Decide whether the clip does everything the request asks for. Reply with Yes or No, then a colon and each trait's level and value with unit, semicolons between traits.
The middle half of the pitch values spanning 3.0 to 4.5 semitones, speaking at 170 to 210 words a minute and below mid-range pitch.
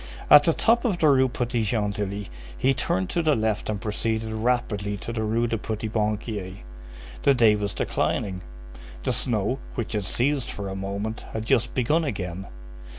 Yes: average, 3.4 semitones; average, 175 wpm; low, 110 Hz